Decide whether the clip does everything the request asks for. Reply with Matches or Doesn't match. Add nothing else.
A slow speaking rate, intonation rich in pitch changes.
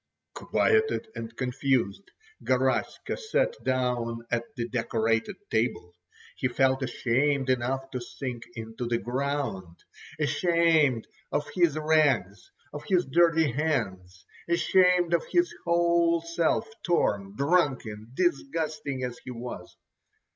Matches